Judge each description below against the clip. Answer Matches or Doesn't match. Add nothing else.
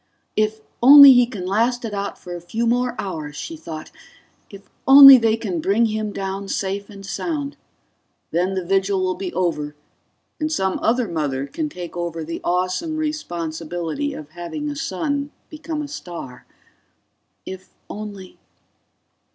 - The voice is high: Matches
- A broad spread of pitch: Matches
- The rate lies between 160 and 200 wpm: Doesn't match